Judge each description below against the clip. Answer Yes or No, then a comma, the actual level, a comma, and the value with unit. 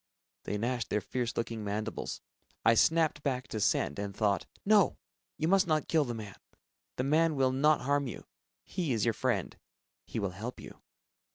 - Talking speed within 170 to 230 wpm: Yes, average, 180 wpm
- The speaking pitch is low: Yes, low, 125 Hz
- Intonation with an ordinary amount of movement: No, wide, 6.1 semitones